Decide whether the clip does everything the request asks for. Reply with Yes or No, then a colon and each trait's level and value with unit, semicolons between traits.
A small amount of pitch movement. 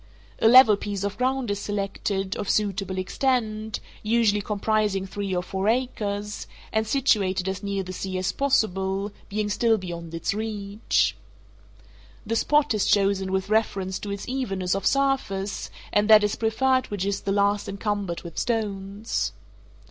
Yes: narrow, 2.3 semitones